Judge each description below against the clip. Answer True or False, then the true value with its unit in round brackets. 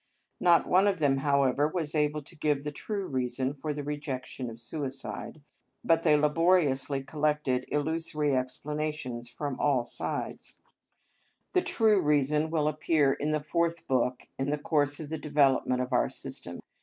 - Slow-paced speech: False (155 wpm)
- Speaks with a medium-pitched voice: True (150 Hz)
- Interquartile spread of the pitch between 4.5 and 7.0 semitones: False (2.4 semitones)